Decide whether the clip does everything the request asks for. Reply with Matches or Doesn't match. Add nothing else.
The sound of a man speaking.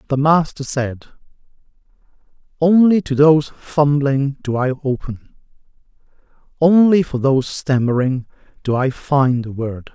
Matches